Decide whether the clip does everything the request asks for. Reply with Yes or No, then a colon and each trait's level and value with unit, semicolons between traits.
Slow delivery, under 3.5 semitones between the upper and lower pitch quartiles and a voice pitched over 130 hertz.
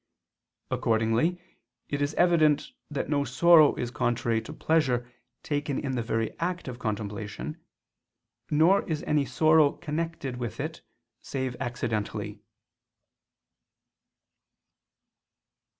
No: slow, 105 wpm; average, 4.9 semitones; medium, 140 Hz